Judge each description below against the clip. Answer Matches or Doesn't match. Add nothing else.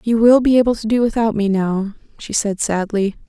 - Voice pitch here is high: Matches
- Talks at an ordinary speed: Doesn't match